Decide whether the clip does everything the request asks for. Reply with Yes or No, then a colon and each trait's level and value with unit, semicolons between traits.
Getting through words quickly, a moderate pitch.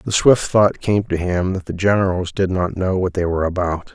No: fast, 245 wpm; very low, 95 Hz